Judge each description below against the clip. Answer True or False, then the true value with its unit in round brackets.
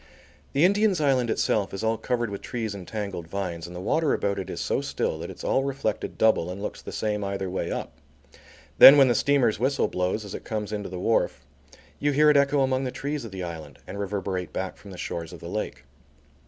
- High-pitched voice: False (105 Hz)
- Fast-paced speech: True (230 wpm)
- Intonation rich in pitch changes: True (5.9 semitones)